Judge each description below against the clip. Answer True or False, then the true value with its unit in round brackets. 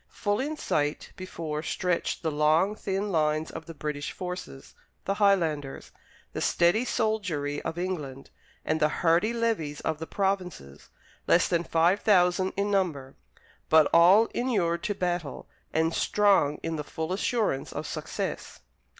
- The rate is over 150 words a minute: False (145 wpm)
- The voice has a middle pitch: True (170 Hz)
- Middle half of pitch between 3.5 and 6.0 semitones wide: True (4.4 semitones)